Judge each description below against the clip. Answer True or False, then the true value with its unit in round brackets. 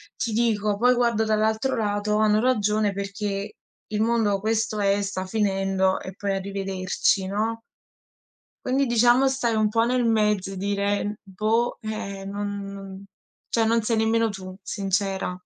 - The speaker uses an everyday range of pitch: False (2.3 semitones)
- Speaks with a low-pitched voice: False (210 Hz)